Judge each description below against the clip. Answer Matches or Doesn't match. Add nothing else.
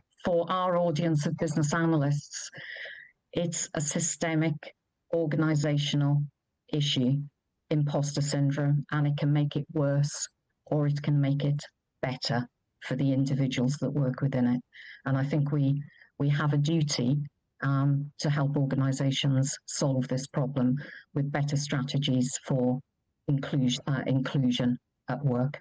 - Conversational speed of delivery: Doesn't match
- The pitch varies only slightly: Matches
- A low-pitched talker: Doesn't match